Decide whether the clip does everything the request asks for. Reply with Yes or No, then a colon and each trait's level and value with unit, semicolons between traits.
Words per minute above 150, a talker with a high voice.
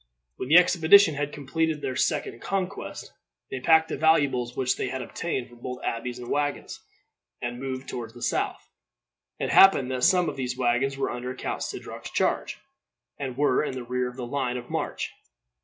No: average, 185 wpm; low, 130 Hz